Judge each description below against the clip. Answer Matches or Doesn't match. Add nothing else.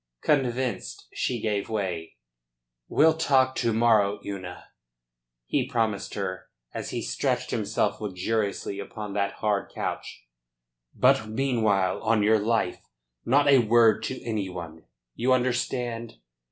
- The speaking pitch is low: Matches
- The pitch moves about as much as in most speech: Matches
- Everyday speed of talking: Doesn't match